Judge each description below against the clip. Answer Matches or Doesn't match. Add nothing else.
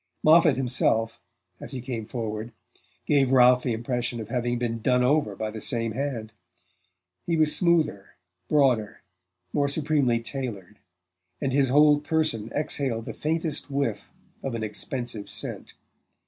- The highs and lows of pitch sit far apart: Doesn't match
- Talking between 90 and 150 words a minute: Matches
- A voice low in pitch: Matches